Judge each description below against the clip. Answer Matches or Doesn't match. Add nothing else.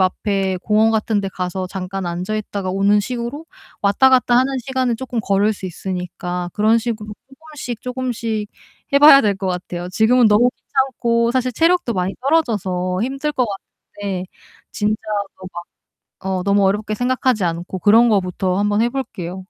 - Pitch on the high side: Matches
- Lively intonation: Doesn't match